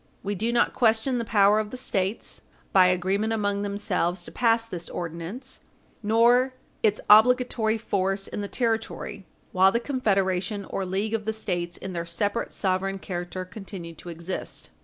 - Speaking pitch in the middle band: No, high, 205 Hz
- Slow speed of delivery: No, average, 160 wpm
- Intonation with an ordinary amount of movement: Yes, average, 3.3 semitones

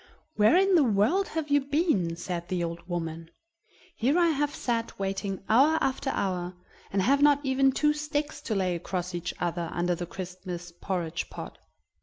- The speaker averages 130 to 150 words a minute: No, average, 175 wpm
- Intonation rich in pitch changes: Yes, wide, 8.4 semitones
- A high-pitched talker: Yes, high, 195 Hz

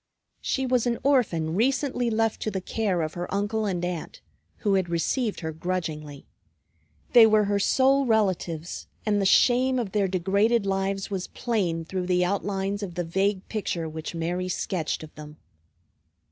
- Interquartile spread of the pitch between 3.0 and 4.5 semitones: Yes, average, 4.1 semitones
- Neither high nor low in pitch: No, high, 195 Hz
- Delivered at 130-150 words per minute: No, average, 165 wpm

